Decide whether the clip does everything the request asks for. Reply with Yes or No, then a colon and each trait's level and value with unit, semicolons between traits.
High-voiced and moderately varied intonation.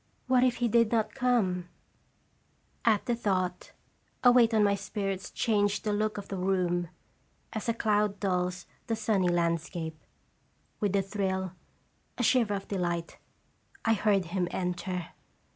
Yes: high, 200 Hz; average, 3.3 semitones